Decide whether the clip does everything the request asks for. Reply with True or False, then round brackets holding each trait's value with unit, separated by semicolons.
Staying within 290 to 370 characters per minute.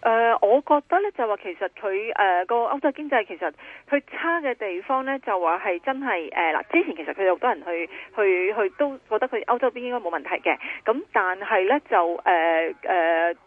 True (300 characters per minute)